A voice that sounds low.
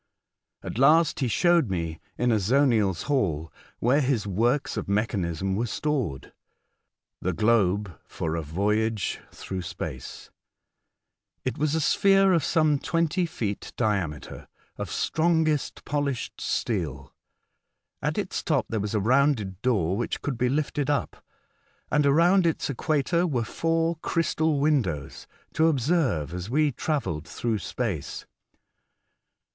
Yes: low, 120 Hz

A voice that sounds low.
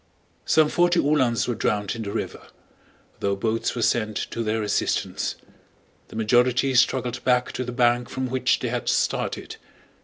Yes: low, 120 Hz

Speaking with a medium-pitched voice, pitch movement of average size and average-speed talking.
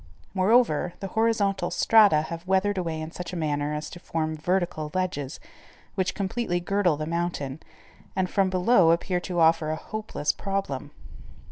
Yes: medium, 175 Hz; average, 3.7 semitones; average, 155 wpm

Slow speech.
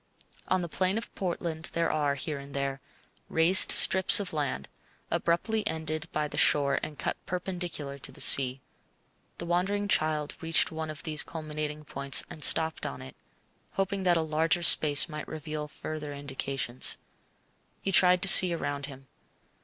No: average, 160 wpm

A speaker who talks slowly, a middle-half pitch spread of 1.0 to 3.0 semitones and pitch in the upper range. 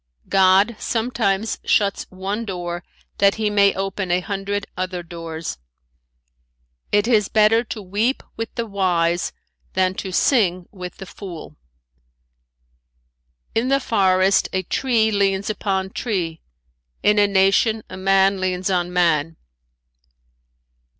Yes: slow, 125 wpm; narrow, 2.5 semitones; high, 195 Hz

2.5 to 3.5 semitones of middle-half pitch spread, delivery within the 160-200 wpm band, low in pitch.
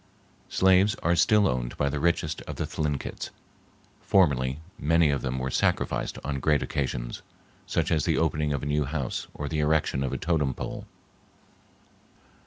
Yes: average, 3.2 semitones; average, 165 wpm; very low, 75 Hz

